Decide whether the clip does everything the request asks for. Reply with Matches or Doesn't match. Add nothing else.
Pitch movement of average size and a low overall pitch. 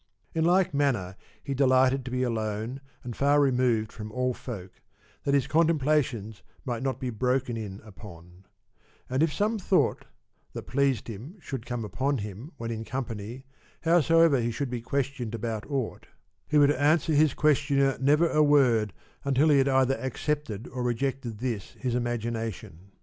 Matches